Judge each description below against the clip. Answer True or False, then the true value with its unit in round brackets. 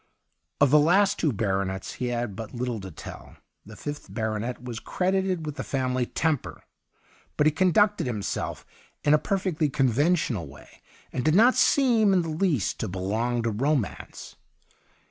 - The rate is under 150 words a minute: False (165 wpm)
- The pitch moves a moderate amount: False (7.3 semitones)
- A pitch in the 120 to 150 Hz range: True (135 Hz)